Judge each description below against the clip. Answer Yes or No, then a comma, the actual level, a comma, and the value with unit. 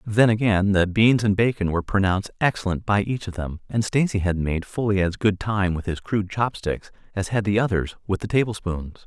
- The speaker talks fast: Yes, fast, 210 wpm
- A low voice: Yes, low, 100 Hz